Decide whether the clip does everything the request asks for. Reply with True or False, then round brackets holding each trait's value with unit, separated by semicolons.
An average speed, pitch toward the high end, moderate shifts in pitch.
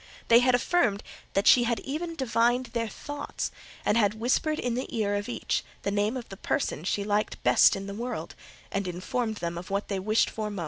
False (210 wpm; 220 Hz; 3.6 semitones)